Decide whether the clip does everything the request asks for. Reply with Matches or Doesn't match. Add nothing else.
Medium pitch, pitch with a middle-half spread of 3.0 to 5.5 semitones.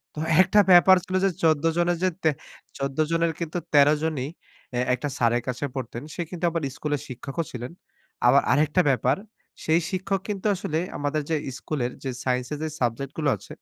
Matches